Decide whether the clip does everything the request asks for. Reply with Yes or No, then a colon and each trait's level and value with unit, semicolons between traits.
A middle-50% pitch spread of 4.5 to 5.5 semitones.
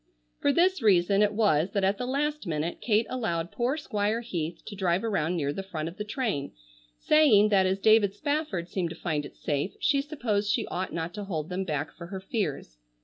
Yes: average, 4.8 semitones